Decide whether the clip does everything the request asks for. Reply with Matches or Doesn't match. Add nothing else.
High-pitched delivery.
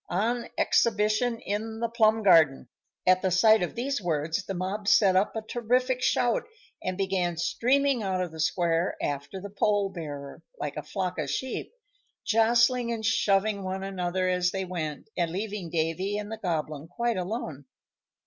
Matches